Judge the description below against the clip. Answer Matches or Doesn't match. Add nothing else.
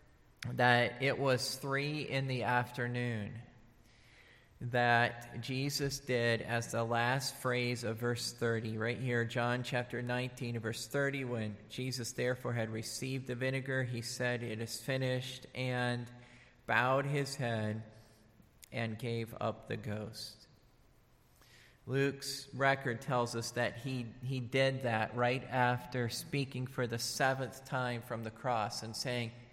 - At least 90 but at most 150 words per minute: Matches